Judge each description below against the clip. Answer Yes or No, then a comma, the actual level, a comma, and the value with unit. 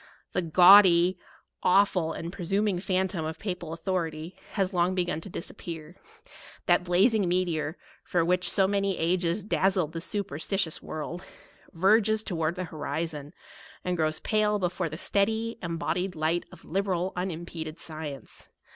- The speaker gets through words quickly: No, average, 145 wpm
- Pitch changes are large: No, average, 2.8 semitones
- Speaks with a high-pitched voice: No, medium, 180 Hz